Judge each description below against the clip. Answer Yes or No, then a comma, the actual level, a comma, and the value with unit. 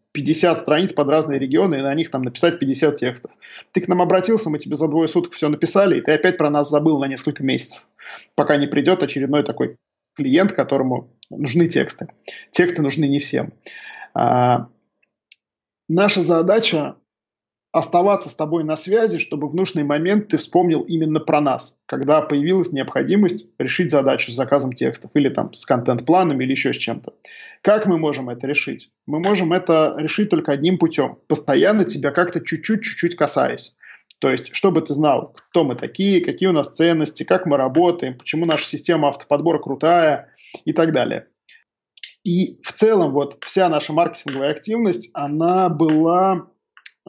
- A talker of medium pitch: Yes, medium, 160 Hz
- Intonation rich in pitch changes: No, average, 3.8 semitones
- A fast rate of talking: Yes, fast, 165 wpm